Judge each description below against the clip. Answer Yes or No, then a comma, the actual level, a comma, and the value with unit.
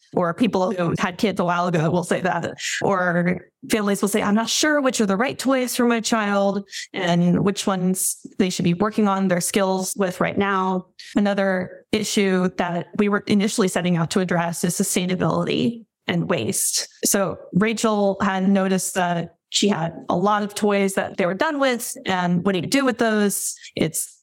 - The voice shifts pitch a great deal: No, average, 2.9 semitones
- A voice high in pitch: Yes, high, 200 Hz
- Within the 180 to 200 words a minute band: Yes, average, 190 wpm